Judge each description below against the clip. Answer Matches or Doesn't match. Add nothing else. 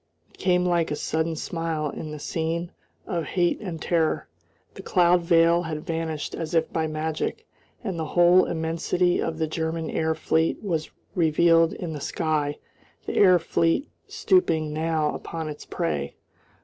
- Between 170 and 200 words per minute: Doesn't match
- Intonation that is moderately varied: Doesn't match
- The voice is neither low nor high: Matches